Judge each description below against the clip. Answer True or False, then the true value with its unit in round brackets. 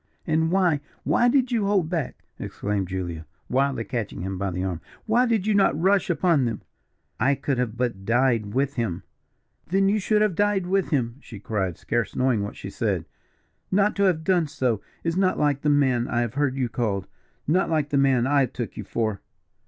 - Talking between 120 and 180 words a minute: False (200 wpm)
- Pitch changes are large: True (8.0 semitones)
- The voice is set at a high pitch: False (140 Hz)